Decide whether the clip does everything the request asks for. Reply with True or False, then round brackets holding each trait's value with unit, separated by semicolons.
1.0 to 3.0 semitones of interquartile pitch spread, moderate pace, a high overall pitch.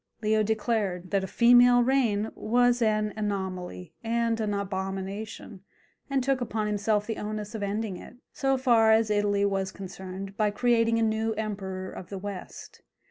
True (2.6 semitones; 160 wpm; 215 Hz)